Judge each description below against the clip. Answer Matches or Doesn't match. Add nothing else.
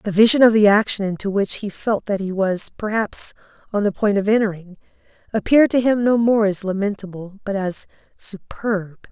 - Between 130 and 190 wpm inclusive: Matches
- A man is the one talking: Doesn't match